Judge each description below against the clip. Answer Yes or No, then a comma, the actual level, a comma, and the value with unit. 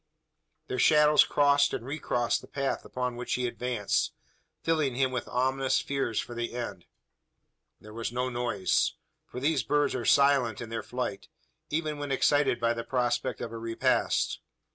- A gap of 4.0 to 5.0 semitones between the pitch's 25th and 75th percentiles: No, average, 3.0 semitones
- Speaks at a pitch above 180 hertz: No, low, 125 Hz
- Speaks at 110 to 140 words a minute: No, average, 165 wpm